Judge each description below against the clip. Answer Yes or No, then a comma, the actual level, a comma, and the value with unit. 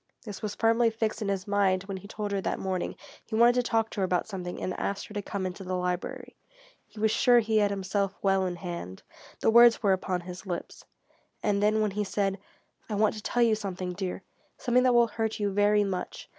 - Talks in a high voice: Yes, high, 200 Hz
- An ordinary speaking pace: No, fast, 230 wpm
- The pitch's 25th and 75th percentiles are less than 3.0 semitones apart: Yes, narrow, 2.6 semitones